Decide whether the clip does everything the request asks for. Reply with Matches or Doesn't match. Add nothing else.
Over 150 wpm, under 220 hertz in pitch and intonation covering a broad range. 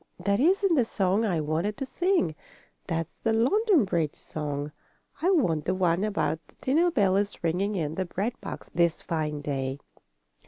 Matches